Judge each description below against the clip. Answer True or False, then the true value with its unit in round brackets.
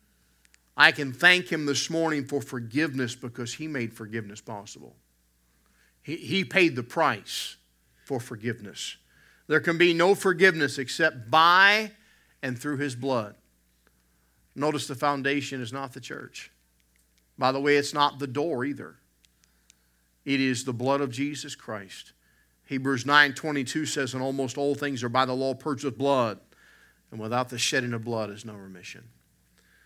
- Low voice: True (130 Hz)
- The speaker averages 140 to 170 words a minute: True (155 wpm)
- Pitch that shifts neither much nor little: False (6.1 semitones)